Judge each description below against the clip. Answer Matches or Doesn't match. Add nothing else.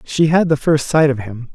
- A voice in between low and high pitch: Matches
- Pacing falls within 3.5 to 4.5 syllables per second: Doesn't match